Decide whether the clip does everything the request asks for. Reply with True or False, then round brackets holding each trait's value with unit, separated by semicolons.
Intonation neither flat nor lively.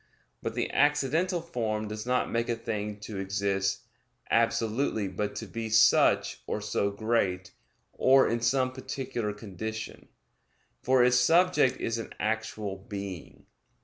True (3.6 semitones)